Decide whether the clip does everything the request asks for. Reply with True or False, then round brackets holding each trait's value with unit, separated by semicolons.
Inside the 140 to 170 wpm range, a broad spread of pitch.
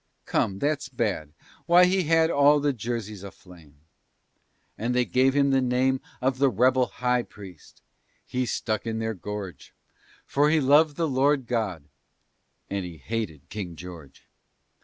True (150 wpm; 5.8 semitones)